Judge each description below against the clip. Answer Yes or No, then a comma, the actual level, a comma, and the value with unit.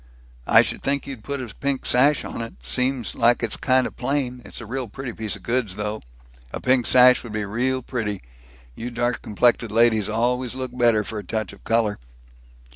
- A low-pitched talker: Yes, low, 120 Hz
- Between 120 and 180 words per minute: No, average, 200 wpm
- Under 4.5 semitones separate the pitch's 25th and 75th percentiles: Yes, average, 2.8 semitones